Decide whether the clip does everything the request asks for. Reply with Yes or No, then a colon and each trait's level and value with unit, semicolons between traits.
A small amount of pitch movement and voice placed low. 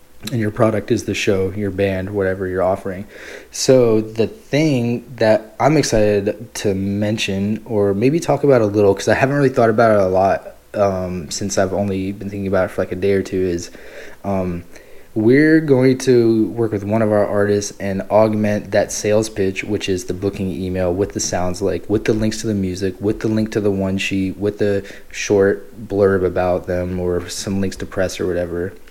Yes: narrow, 2.3 semitones; low, 100 Hz